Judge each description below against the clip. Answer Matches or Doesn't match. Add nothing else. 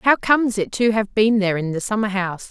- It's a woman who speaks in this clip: Matches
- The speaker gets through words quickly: Matches